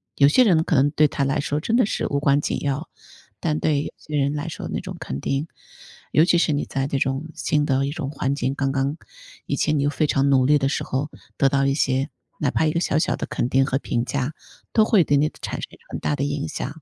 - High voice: No, medium, 145 Hz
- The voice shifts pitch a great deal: No, narrow, 1.8 semitones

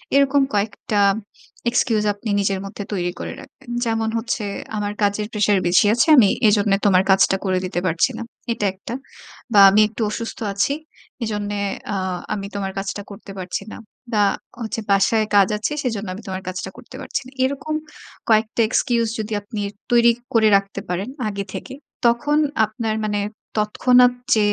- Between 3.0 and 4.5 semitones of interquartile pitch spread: No, narrow, 2.6 semitones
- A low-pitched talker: No, high, 210 Hz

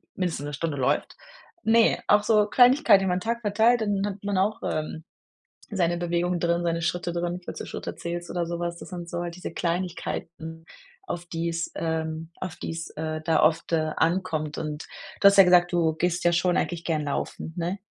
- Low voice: No, medium, 175 Hz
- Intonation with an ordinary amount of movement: No, narrow, 2.3 semitones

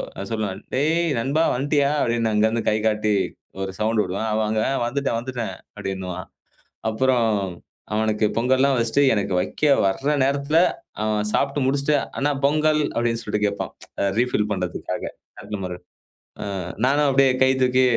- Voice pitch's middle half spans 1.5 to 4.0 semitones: No, average, 4.5 semitones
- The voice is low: Yes, low, 115 Hz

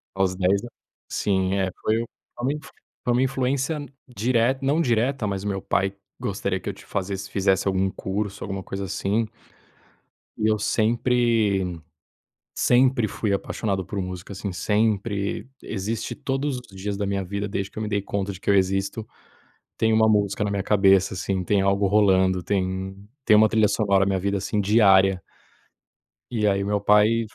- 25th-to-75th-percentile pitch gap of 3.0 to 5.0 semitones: No, narrow, 2.4 semitones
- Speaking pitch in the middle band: No, low, 100 Hz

